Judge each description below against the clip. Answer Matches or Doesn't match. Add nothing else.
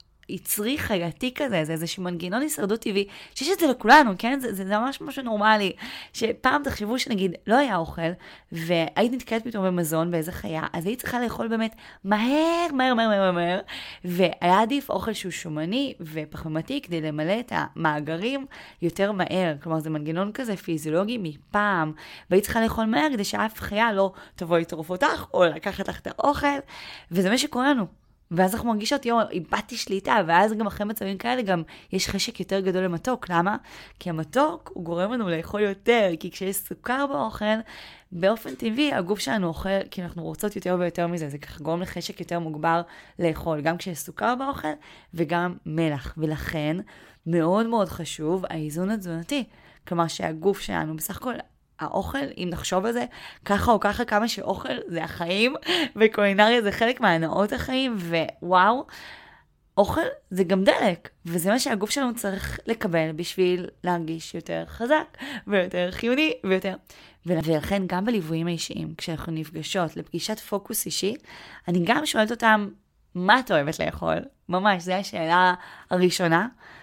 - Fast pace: Matches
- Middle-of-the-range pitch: Doesn't match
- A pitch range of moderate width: Matches